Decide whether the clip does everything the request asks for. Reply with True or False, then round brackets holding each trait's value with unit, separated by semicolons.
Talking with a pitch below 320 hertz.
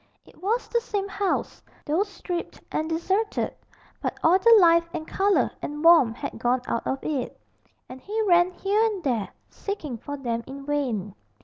False (335 Hz)